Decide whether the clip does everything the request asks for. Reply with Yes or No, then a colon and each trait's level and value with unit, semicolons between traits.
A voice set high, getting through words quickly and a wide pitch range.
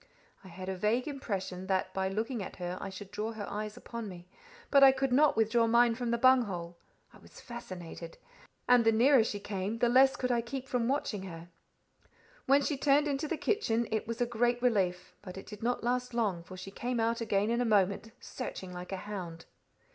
No: high, 225 Hz; fast, 215 wpm; average, 4.5 semitones